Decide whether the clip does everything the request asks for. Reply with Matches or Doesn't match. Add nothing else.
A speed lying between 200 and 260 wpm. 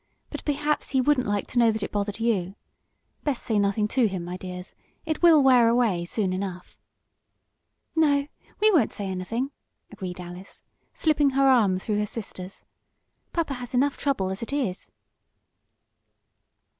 Doesn't match